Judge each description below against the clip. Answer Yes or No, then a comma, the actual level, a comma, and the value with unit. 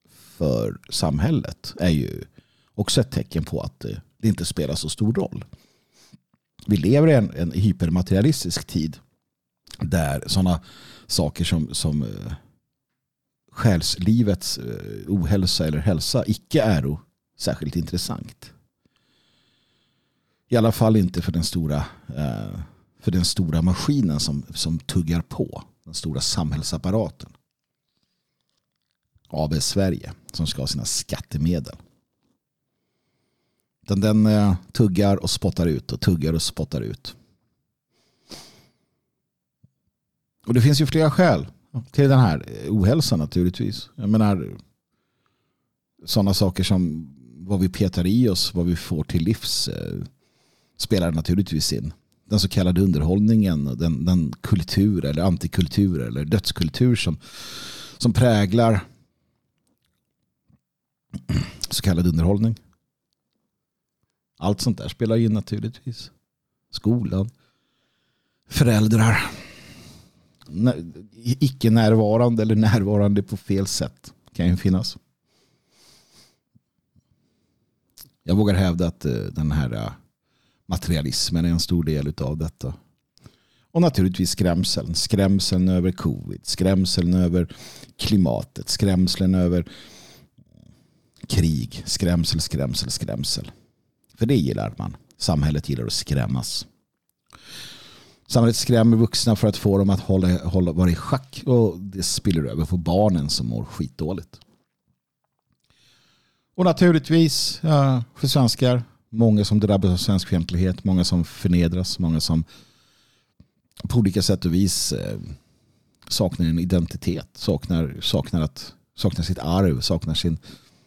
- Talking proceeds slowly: Yes, slow, 115 wpm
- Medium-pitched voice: No, very low, 95 Hz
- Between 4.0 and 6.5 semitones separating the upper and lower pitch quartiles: Yes, average, 4.4 semitones